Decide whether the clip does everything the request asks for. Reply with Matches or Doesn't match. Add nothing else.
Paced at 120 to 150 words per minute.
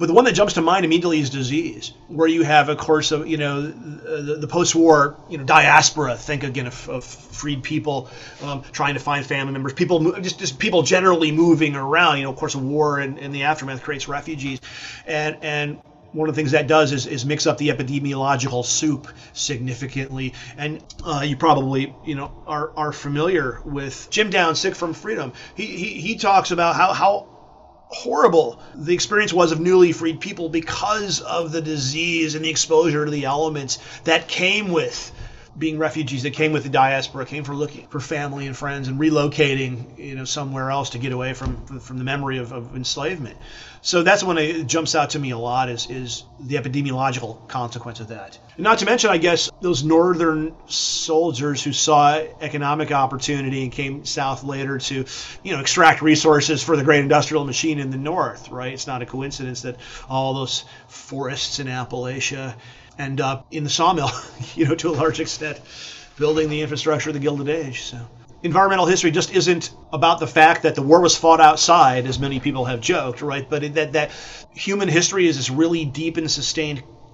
Doesn't match